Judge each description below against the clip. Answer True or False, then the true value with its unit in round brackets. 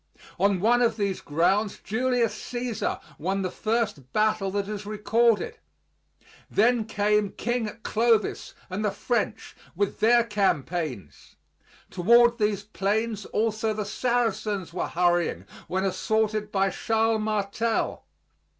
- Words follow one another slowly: True (120 wpm)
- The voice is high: True (210 Hz)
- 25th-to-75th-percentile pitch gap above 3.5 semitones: False (2.5 semitones)